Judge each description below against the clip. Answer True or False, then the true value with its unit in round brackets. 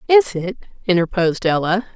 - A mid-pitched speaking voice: False (200 Hz)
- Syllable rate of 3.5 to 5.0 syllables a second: False (5.6 syllables/s)